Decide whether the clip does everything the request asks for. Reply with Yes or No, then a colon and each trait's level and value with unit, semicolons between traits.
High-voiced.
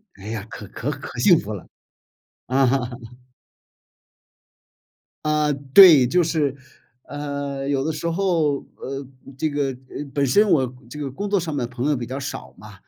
No: medium, 145 Hz